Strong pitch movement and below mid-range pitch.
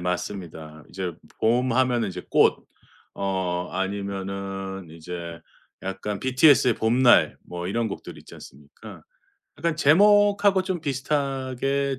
Yes: wide, 6.6 semitones; low, 105 Hz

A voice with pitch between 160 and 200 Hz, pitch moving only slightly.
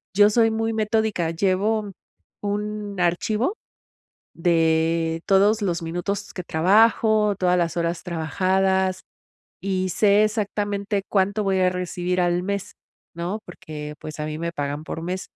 No: high, 190 Hz; average, 3.4 semitones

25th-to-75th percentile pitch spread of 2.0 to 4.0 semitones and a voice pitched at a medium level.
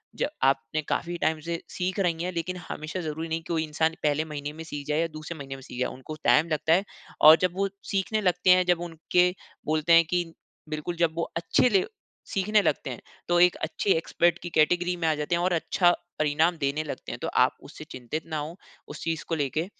Yes: narrow, 2.5 semitones; medium, 165 Hz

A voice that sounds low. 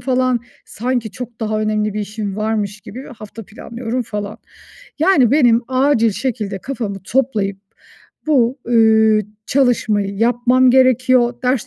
No: high, 230 Hz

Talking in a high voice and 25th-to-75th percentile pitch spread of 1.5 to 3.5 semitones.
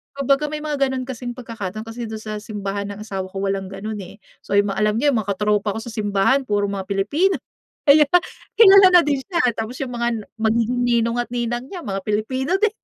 No: high, 230 Hz; average, 4.4 semitones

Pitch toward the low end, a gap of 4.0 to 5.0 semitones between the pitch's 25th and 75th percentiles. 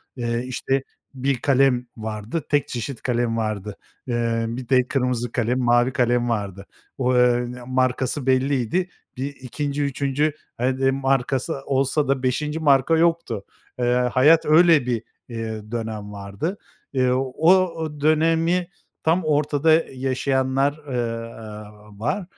No: low, 130 Hz; average, 3.4 semitones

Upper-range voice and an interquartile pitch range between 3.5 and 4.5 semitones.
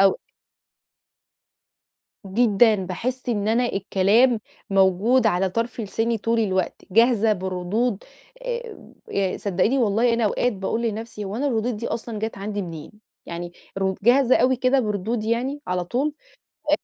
Yes: high, 220 Hz; average, 3.8 semitones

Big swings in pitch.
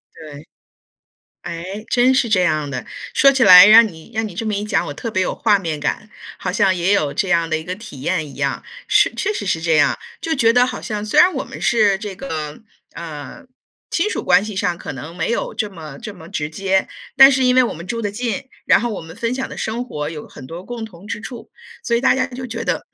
Yes: wide, 6.2 semitones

